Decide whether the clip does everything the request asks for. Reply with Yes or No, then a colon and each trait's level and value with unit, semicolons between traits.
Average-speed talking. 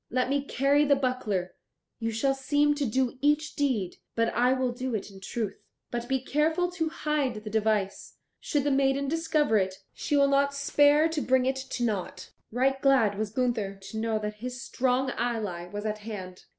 Yes: average, 190 wpm